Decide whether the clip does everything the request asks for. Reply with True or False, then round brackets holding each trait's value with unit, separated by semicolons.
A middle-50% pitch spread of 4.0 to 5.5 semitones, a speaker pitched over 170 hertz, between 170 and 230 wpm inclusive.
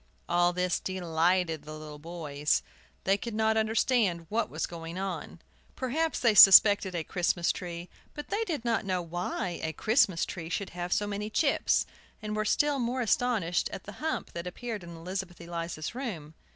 True (4.5 semitones; 185 Hz; 175 wpm)